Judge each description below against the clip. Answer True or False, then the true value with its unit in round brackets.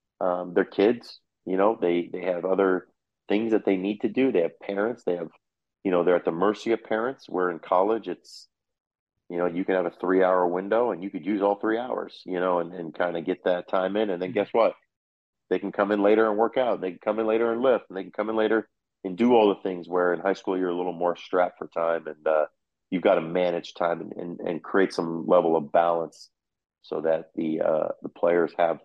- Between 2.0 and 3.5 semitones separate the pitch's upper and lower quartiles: True (2.8 semitones)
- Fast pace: True (255 wpm)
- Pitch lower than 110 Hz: True (90 Hz)